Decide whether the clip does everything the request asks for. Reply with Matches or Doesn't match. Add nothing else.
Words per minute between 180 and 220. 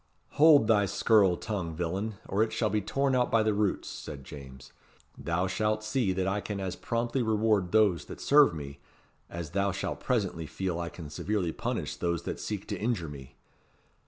Matches